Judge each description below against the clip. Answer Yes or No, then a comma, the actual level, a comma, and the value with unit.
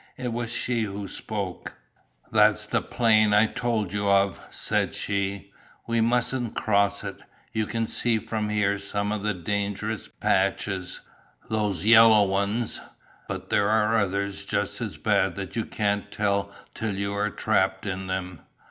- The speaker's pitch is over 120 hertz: No, low, 105 Hz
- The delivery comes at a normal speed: Yes, average, 155 wpm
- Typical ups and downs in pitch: No, narrow, 1.8 semitones